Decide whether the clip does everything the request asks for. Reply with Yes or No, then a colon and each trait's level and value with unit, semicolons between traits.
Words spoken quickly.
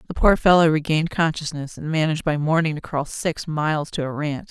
Yes: fast, 215 wpm